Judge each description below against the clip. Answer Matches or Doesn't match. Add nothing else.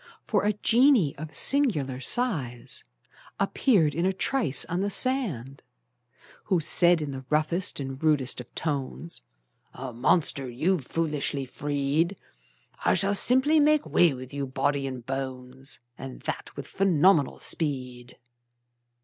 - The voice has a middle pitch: Matches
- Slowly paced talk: Matches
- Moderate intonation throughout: Doesn't match